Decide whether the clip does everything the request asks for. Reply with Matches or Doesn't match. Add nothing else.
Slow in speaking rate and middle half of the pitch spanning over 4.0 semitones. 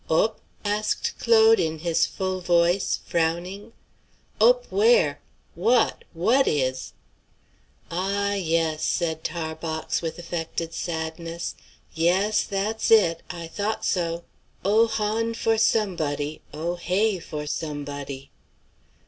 Matches